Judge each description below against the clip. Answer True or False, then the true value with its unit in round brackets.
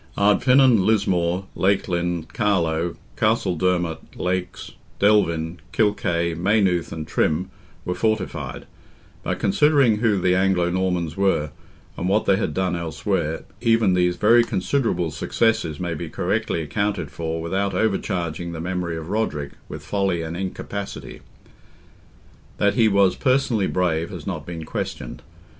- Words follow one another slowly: True (130 wpm)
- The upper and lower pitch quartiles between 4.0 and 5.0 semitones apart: False (3.4 semitones)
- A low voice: True (90 Hz)